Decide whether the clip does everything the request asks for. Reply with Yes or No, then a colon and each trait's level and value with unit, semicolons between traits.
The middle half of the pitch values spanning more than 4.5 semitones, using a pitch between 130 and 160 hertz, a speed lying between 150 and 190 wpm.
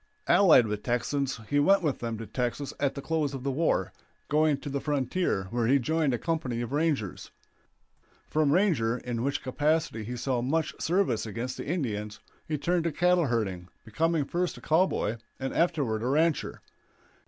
Yes: average, 5.1 semitones; medium, 140 Hz; average, 175 wpm